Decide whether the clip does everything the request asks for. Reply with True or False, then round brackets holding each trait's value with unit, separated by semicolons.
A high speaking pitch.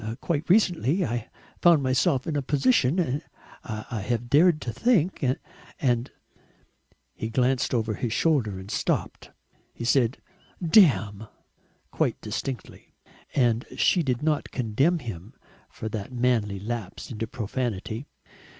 False (125 Hz)